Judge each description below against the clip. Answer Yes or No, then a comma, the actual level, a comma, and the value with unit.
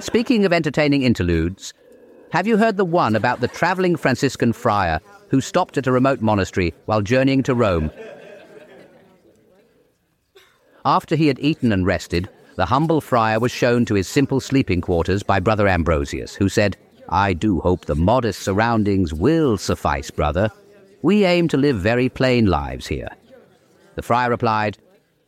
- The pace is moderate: Yes, average, 155 wpm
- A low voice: Yes, low, 115 Hz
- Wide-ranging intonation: Yes, wide, 7.1 semitones